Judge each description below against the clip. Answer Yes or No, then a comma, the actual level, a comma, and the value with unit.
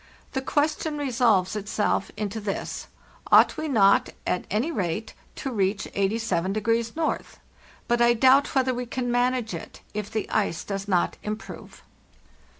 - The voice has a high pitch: Yes, high, 220 Hz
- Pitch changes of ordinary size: Yes, average, 4.2 semitones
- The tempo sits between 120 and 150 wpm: Yes, average, 145 wpm